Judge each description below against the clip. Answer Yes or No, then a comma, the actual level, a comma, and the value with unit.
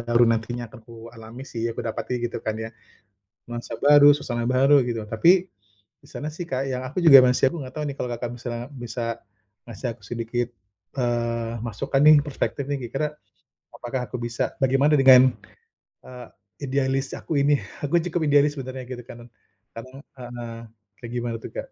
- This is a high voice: No, low, 125 Hz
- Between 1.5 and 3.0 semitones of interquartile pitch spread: Yes, average, 2.7 semitones